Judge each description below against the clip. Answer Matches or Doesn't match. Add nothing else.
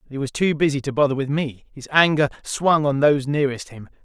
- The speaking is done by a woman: Doesn't match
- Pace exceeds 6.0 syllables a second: Matches